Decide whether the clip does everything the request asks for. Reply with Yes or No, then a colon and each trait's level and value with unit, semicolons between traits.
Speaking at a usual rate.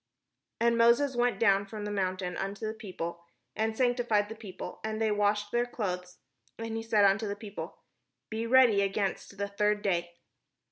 Yes: average, 185 wpm